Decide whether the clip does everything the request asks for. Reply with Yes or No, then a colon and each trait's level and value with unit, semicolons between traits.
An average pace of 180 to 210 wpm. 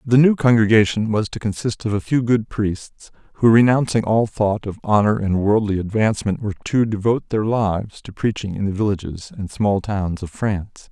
Yes: average, 190 wpm